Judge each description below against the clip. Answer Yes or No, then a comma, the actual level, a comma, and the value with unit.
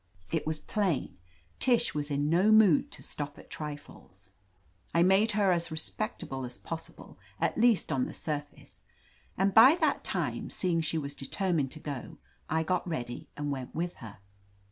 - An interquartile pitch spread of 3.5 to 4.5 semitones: No, average, 4.9 semitones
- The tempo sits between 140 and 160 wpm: No, average, 170 wpm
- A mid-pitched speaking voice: Yes, medium, 160 Hz